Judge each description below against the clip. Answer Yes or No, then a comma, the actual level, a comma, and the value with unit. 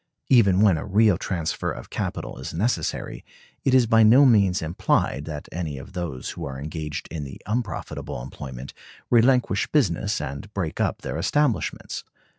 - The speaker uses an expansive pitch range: Yes, wide, 6.8 semitones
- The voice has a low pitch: Yes, very low, 90 Hz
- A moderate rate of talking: Yes, average, 160 wpm